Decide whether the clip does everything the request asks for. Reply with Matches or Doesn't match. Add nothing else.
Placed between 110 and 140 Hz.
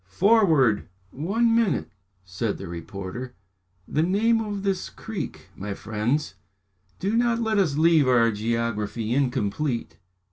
Matches